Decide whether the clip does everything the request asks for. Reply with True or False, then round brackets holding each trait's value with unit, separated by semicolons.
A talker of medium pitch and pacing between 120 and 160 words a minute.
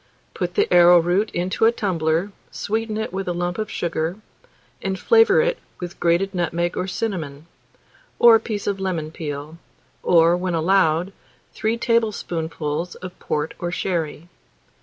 True (180 Hz; 140 wpm)